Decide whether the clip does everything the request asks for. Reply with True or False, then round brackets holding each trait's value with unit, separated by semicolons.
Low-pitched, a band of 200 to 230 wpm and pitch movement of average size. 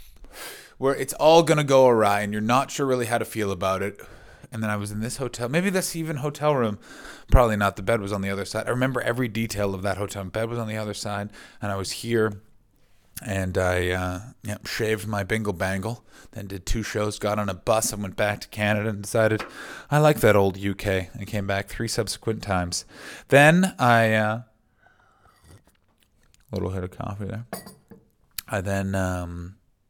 True (105 Hz; 205 wpm; 3.1 semitones)